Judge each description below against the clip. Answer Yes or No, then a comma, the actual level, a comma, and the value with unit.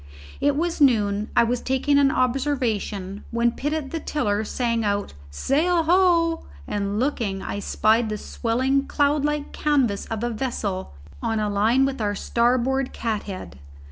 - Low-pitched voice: No, high, 240 Hz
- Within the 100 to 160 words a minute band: Yes, average, 155 wpm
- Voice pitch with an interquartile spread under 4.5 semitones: No, average, 5.2 semitones